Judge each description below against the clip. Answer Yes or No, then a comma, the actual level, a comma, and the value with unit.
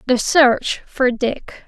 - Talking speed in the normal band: Yes, average, 145 wpm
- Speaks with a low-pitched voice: No, very high, 255 Hz